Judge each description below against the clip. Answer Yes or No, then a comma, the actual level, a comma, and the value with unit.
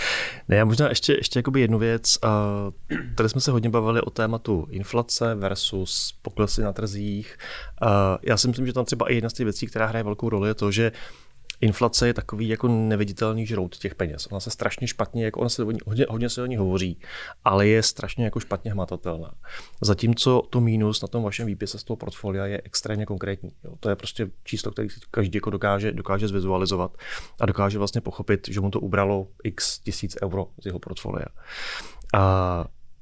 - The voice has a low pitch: Yes, low, 110 Hz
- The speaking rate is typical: No, fast, 190 wpm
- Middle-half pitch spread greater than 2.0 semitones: Yes, average, 2.7 semitones